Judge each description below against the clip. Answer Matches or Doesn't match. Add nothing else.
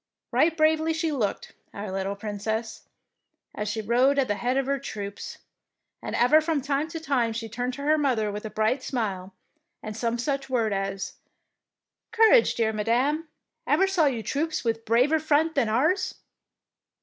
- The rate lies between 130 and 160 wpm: Doesn't match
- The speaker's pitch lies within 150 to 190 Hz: Doesn't match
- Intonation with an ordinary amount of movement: Doesn't match